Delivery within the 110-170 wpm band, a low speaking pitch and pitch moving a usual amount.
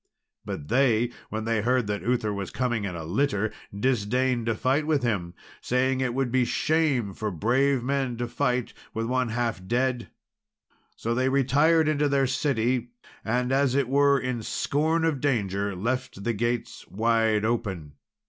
Yes: average, 165 wpm; low, 120 Hz; average, 3.3 semitones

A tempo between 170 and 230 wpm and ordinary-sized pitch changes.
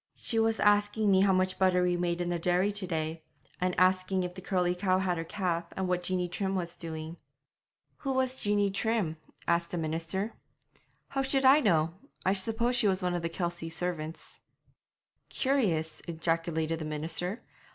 Yes: average, 180 wpm; average, 3.3 semitones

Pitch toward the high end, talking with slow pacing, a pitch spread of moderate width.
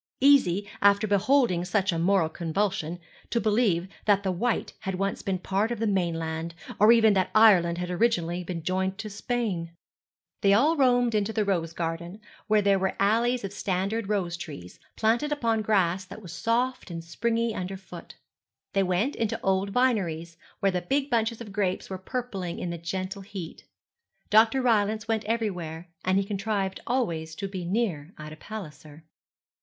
No: high, 195 Hz; average, 175 wpm; average, 4.1 semitones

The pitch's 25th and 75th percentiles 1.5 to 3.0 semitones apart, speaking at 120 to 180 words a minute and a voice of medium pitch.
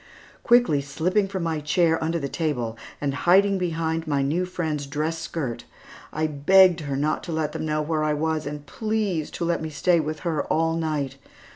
No: narrow, 2.4 semitones; average, 190 wpm; medium, 160 Hz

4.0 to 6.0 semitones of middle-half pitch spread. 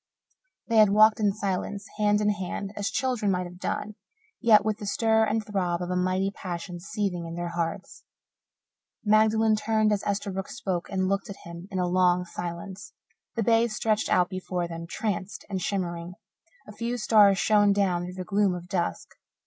No: average, 2.9 semitones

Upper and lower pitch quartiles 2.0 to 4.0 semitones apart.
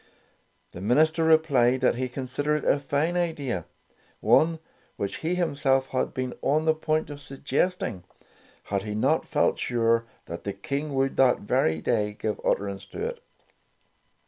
No: average, 5.3 semitones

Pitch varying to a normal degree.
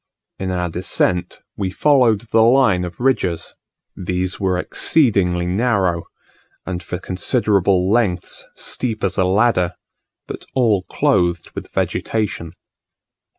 Yes: average, 3.9 semitones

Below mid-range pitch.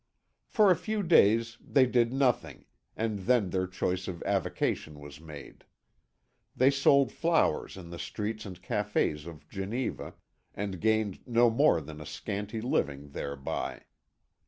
Yes: low, 105 Hz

